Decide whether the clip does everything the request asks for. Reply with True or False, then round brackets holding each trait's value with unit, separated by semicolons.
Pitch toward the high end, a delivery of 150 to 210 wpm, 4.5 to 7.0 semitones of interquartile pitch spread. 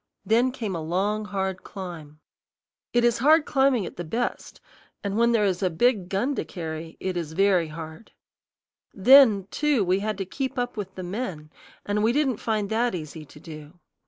True (200 Hz; 190 wpm; 5.3 semitones)